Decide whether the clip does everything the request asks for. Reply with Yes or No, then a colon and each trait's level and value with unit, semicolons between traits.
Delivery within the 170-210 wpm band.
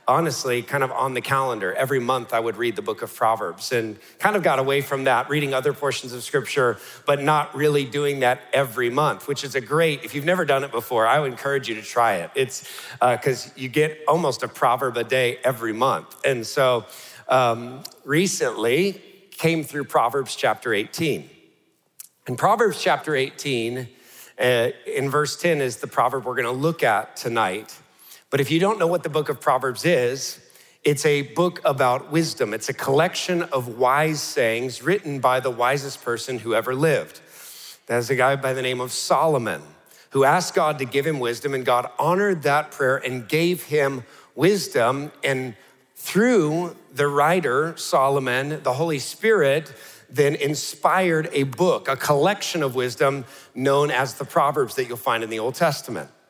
Yes: average, 180 wpm